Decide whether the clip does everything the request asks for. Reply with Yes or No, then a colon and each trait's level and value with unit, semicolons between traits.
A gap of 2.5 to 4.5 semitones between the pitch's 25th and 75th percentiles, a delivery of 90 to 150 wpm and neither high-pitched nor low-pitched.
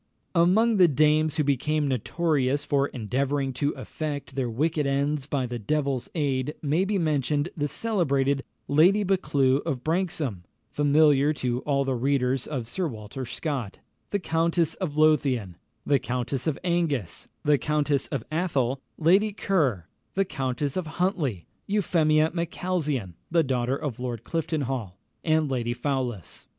Yes: average, 3.7 semitones; average, 140 wpm; medium, 145 Hz